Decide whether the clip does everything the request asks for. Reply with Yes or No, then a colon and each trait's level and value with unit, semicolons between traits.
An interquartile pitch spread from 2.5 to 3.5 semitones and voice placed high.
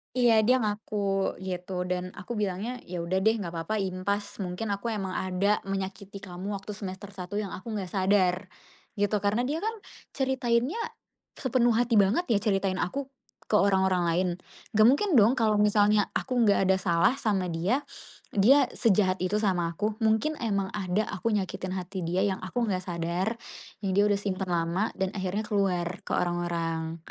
Yes: average, 2.9 semitones; high, 200 Hz